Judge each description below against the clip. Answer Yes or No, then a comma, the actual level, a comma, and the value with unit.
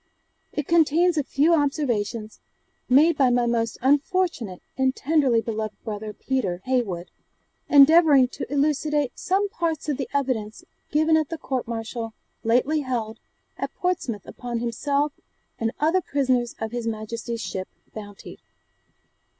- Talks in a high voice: Yes, very high, 260 Hz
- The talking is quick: No, slow, 135 wpm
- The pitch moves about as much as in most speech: Yes, average, 4.8 semitones